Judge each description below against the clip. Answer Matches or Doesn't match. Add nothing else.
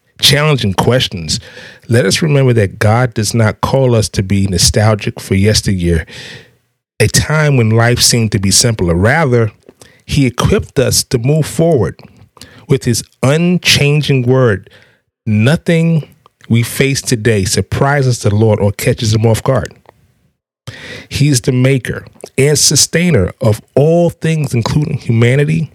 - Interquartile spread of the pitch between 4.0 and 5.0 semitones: Matches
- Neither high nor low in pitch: Doesn't match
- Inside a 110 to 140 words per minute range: Matches